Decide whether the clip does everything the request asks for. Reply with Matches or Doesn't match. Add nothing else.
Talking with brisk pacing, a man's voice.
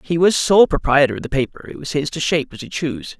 Matches